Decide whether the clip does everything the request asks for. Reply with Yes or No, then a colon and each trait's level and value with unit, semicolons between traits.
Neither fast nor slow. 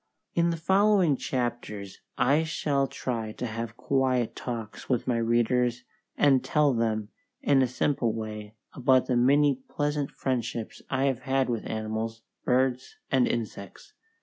Yes: average, 145 wpm